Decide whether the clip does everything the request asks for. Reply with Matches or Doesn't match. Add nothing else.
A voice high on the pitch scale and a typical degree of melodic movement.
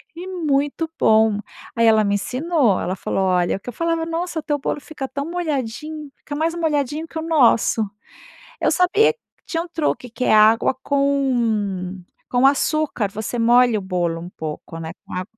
Doesn't match